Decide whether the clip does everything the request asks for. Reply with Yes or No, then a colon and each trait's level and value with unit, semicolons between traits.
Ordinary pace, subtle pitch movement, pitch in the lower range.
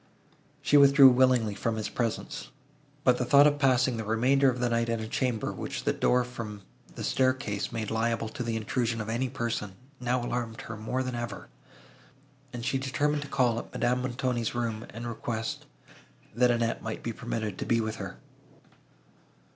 Yes: average, 180 wpm; narrow, 2.3 semitones; low, 120 Hz